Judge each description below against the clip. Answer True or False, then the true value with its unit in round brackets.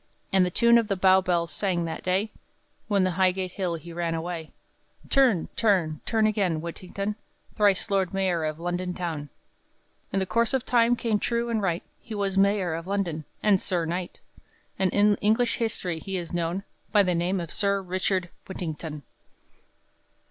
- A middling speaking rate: True (170 wpm)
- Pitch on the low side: False (185 Hz)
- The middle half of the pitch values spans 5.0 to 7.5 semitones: False (3.0 semitones)